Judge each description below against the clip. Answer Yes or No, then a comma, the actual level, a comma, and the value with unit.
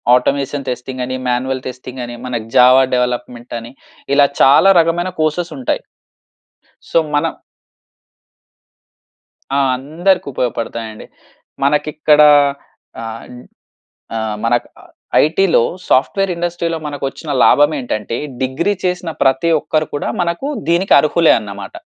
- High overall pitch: No, medium, 140 Hz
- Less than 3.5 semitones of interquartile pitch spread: No, average, 5.1 semitones